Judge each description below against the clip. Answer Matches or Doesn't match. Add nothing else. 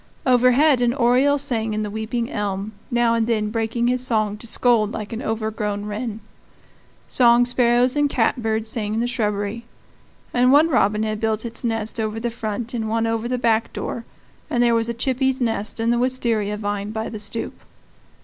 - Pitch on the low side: Doesn't match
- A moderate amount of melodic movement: Doesn't match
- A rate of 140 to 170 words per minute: Doesn't match